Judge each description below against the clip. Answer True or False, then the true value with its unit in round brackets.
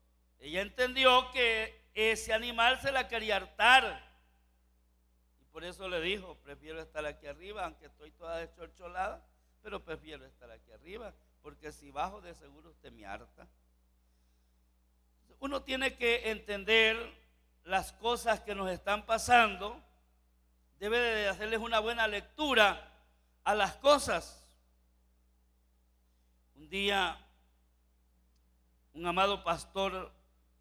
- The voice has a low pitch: False (160 Hz)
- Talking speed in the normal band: False (115 wpm)